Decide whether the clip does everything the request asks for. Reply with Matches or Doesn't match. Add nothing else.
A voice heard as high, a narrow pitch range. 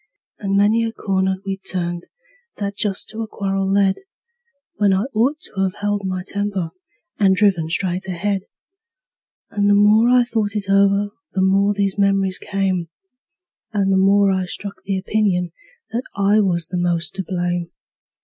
Matches